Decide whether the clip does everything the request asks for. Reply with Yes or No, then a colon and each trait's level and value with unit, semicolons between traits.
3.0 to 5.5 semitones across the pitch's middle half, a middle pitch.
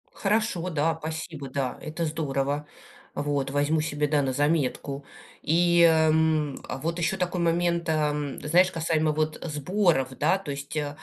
No: narrow, 2.6 semitones; medium, 155 Hz